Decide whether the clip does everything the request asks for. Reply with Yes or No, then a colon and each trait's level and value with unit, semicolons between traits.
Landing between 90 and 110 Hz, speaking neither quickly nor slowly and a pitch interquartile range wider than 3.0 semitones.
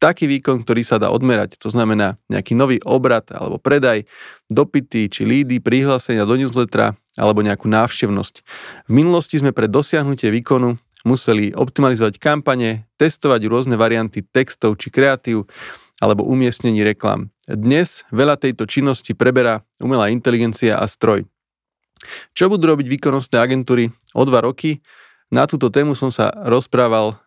No: low, 125 Hz; average, 140 wpm; average, 3.5 semitones